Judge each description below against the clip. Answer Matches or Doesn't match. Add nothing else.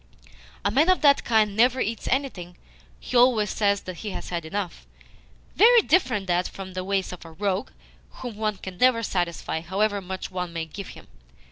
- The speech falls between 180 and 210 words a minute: Matches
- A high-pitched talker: Matches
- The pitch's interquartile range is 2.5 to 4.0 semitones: Doesn't match